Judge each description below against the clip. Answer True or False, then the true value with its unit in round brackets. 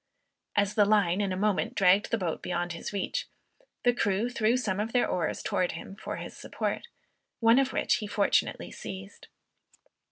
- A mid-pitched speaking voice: False (205 Hz)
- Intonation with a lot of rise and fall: False (3.2 semitones)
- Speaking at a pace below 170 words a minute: False (180 wpm)